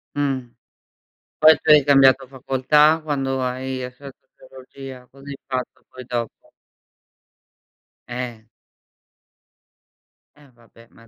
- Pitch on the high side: No, low, 130 Hz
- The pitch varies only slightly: Yes, narrow, 1.7 semitones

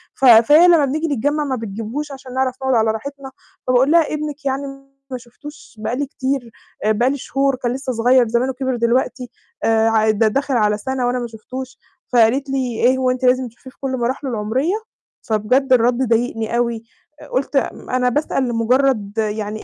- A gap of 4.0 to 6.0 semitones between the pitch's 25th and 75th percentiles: No, average, 3.0 semitones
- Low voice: No, very high, 255 Hz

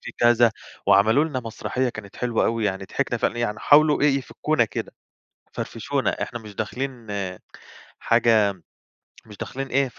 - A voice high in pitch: No, low, 120 Hz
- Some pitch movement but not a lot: Yes, average, 3.8 semitones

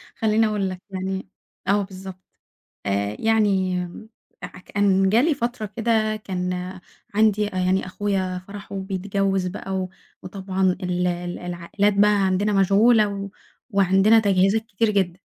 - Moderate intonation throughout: No, narrow, 2.1 semitones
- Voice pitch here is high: Yes, high, 195 Hz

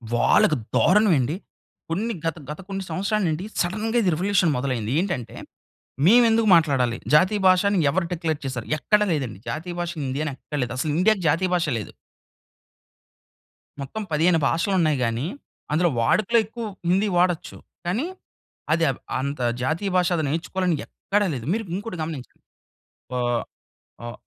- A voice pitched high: No, medium, 170 Hz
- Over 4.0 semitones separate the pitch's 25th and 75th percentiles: Yes, wide, 5.4 semitones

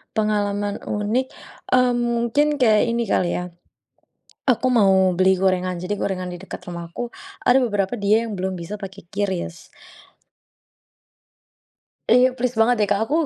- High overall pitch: Yes, high, 205 Hz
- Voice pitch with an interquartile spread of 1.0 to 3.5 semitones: No, average, 4.1 semitones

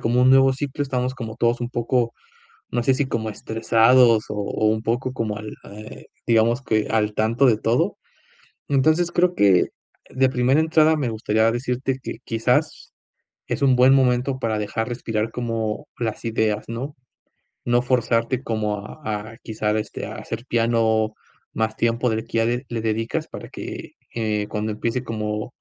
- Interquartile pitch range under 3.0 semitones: Yes, narrow, 2.6 semitones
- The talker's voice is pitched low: Yes, low, 115 Hz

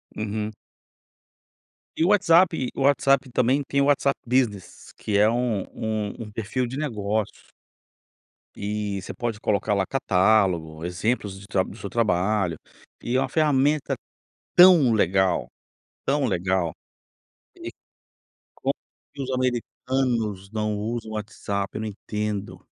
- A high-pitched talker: No, low, 110 Hz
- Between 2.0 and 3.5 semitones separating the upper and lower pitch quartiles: No, average, 4.6 semitones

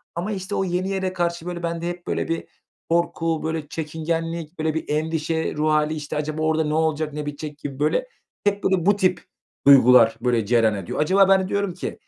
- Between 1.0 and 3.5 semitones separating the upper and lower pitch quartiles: Yes, average, 2.9 semitones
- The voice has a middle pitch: Yes, medium, 160 Hz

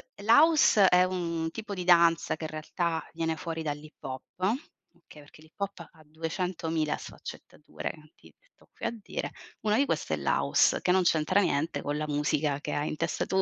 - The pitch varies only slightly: No, average, 3.3 semitones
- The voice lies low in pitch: No, medium, 165 Hz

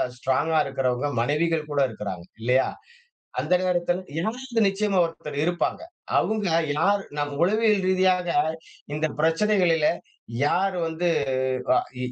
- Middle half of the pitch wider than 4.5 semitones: Yes, average, 4.9 semitones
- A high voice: No, medium, 170 Hz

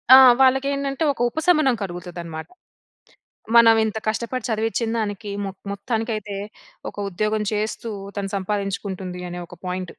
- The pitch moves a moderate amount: Yes, average, 3.5 semitones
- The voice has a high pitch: Yes, high, 215 Hz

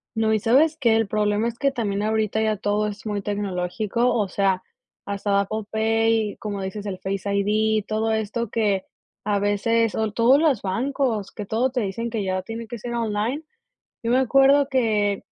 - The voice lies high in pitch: Yes, high, 220 Hz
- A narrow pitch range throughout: Yes, narrow, 2.3 semitones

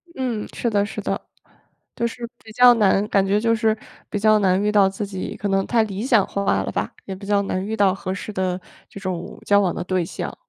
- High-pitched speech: Yes, high, 200 Hz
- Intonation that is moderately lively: No, narrow, 2.3 semitones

